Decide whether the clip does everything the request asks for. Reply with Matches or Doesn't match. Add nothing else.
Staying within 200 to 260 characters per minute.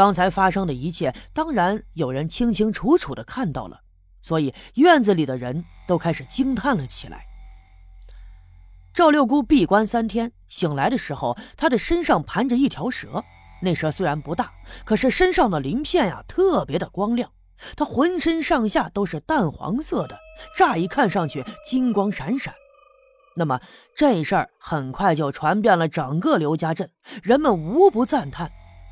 Matches